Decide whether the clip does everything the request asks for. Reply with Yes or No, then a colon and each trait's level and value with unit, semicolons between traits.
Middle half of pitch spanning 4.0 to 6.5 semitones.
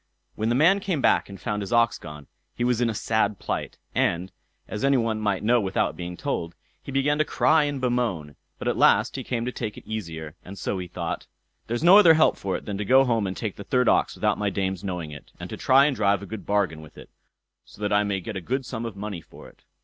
Yes: average, 4.8 semitones